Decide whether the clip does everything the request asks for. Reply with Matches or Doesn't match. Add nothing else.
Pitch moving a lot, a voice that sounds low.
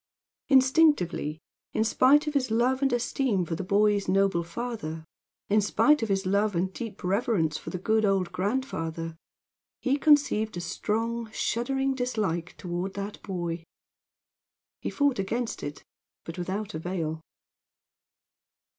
Doesn't match